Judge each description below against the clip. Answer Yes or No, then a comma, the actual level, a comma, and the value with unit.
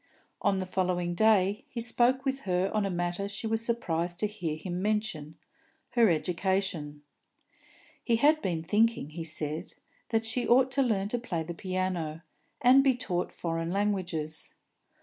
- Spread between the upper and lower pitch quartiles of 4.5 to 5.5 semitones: Yes, average, 4.8 semitones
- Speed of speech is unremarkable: Yes, average, 160 wpm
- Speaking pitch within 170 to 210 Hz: Yes, high, 190 Hz